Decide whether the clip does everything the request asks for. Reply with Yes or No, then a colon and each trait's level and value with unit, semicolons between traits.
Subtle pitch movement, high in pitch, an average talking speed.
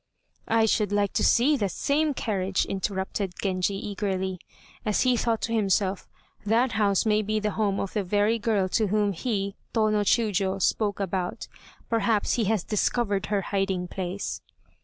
Yes: narrow, 2.2 semitones; high, 205 Hz; average, 160 wpm